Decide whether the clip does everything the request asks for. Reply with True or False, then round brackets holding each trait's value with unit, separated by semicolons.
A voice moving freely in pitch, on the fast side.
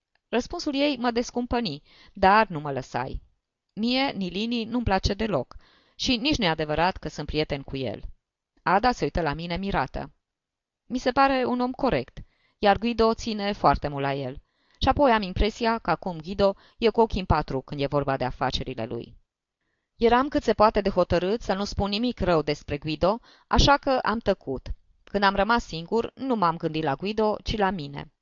True (7.6 semitones; 185 wpm)